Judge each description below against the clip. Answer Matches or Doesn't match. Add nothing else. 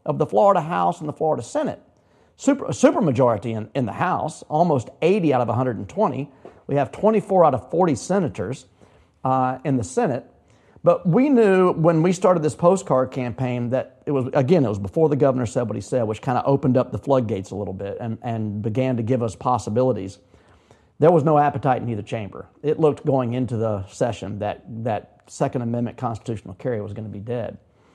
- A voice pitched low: Matches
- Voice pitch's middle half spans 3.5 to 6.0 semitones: Matches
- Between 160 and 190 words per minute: Doesn't match